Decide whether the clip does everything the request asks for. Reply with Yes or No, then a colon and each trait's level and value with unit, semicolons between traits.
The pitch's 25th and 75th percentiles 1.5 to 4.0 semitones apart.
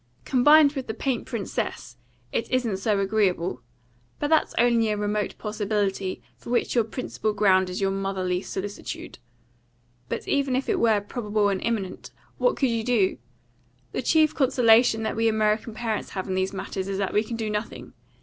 Yes: average, 3.3 semitones